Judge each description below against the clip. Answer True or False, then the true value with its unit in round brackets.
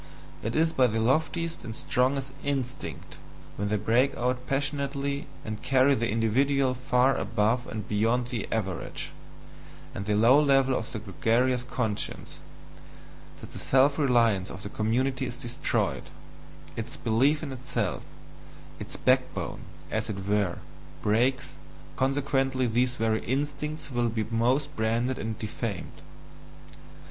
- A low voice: True (125 Hz)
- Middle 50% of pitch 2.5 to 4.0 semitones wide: True (3.6 semitones)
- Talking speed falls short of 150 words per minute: True (135 wpm)